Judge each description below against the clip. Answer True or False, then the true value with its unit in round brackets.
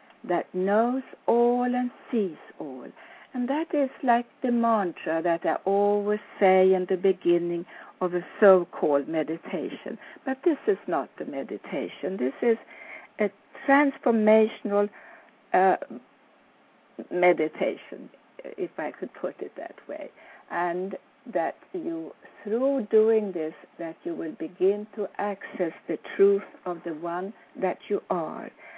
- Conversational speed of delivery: False (130 wpm)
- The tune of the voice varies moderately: False (5.8 semitones)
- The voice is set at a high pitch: True (205 Hz)